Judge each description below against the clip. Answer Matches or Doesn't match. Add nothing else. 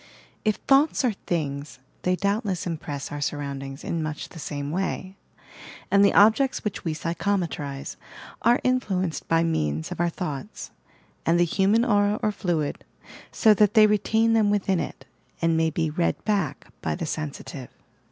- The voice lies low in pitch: Doesn't match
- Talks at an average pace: Matches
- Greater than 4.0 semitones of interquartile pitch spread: Matches